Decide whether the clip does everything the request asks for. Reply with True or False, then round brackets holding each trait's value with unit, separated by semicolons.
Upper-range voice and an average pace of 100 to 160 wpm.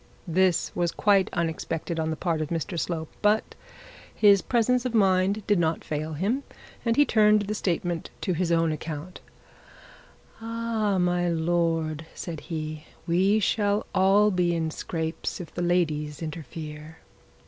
False (175 Hz; 150 wpm)